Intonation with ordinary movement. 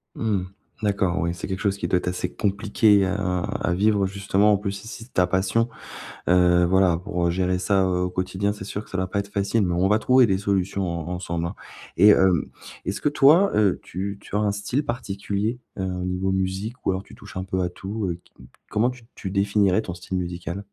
No: narrow, 2.2 semitones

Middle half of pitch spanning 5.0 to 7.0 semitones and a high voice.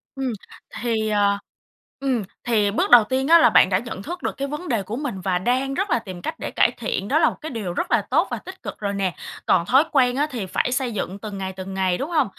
Yes: wide, 5.6 semitones; high, 225 Hz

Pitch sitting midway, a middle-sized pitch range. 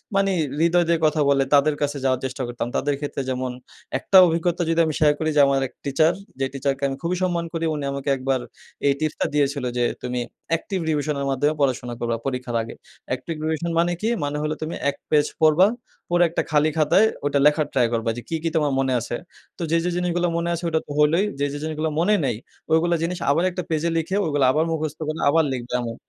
Yes: medium, 150 Hz; average, 3.5 semitones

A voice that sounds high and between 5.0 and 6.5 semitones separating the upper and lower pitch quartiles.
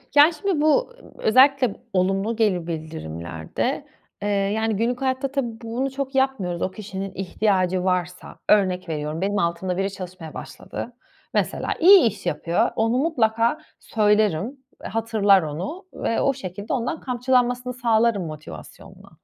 Yes: high, 215 Hz; wide, 5.5 semitones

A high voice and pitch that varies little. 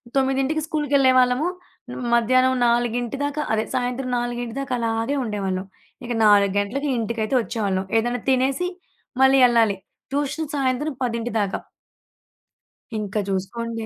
No: high, 240 Hz; average, 3.2 semitones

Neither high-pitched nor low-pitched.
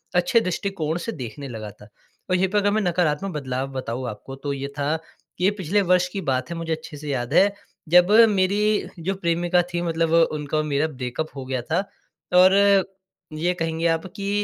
Yes: medium, 165 Hz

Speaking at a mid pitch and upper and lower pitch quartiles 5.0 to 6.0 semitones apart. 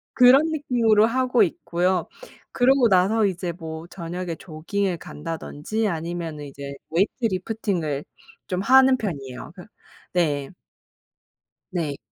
Yes: medium, 180 Hz; wide, 5.5 semitones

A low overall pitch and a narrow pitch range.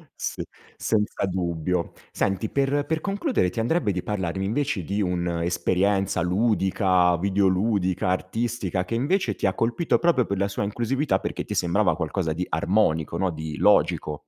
No: very low, 95 Hz; average, 4.2 semitones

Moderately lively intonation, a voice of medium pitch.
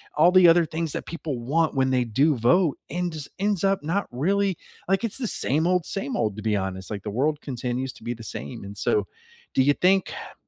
No: wide, 6.8 semitones; medium, 145 Hz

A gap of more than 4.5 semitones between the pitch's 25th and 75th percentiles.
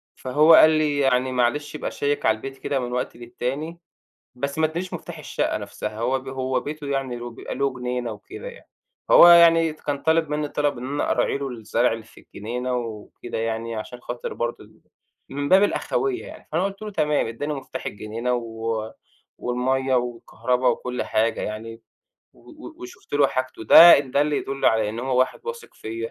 No: average, 4.0 semitones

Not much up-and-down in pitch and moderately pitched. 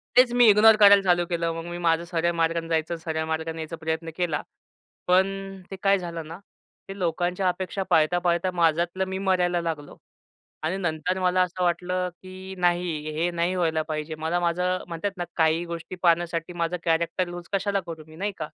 Yes: narrow, 1.9 semitones; medium, 175 Hz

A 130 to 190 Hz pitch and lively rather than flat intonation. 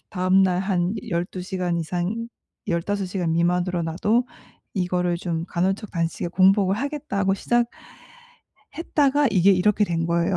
No: medium, 185 Hz; average, 3.1 semitones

